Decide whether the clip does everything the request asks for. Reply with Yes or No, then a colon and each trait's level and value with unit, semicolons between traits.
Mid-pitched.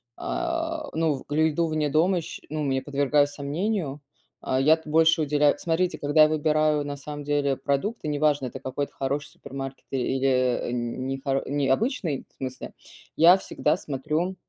Yes: medium, 145 Hz